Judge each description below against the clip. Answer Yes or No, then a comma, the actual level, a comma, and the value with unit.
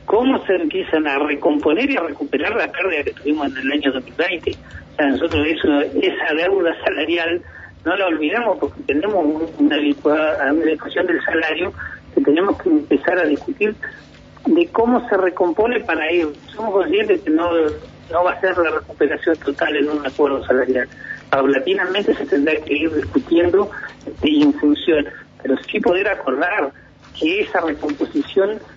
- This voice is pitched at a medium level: Yes, medium, 175 Hz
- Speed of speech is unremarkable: Yes, average, 160 wpm